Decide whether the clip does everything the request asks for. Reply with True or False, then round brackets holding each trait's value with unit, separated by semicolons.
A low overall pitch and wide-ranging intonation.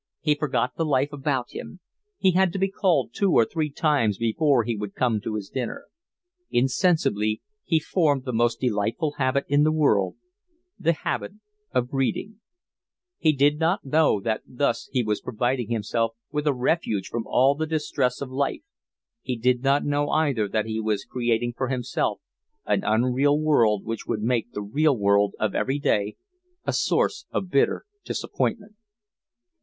False (130 Hz; 4.9 semitones)